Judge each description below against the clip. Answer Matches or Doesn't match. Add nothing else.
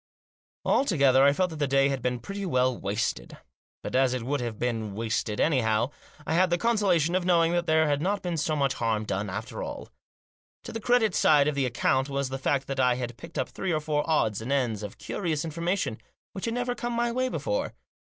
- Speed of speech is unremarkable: Doesn't match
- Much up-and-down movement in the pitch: Matches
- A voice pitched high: Doesn't match